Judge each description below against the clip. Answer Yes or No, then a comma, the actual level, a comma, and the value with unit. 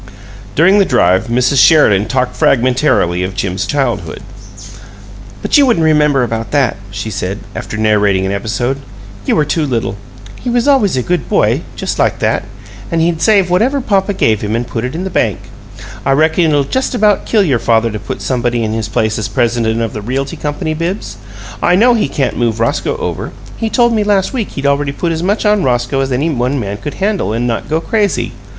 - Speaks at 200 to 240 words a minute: Yes, fast, 205 wpm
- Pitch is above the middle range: No, low, 135 Hz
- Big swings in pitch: Yes, wide, 7.8 semitones